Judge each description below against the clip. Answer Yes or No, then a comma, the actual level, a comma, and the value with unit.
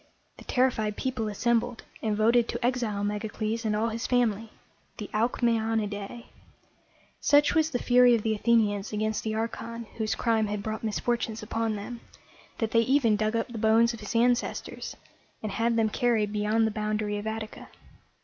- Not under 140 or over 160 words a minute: No, average, 180 wpm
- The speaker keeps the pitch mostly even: Yes, narrow, 1.8 semitones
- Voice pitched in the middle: No, high, 225 Hz